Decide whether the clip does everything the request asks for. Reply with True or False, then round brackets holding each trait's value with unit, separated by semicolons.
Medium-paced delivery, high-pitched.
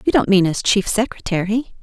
True (195 wpm; 210 Hz)